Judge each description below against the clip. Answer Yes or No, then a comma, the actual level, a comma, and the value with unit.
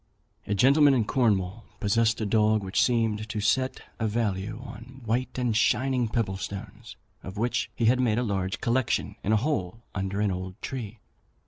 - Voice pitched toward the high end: No, low, 110 Hz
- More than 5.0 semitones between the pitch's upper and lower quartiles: No, average, 3.3 semitones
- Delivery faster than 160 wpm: Yes, average, 180 wpm